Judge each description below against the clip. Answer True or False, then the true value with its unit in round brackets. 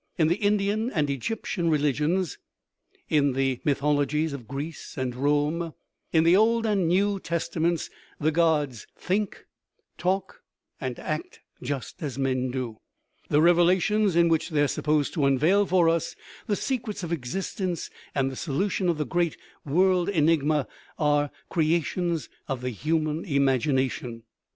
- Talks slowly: False (150 wpm)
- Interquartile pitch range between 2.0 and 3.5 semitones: False (4.1 semitones)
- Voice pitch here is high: False (155 Hz)